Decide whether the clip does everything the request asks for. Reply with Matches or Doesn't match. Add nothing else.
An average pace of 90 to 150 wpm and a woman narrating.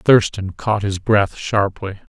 Doesn't match